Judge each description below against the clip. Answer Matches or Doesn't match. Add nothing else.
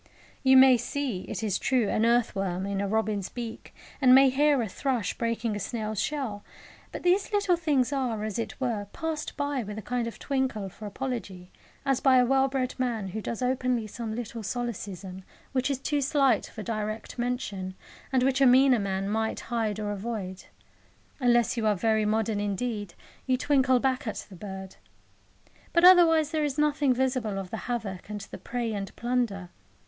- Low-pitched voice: Doesn't match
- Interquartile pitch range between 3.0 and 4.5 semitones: Matches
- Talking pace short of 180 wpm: Doesn't match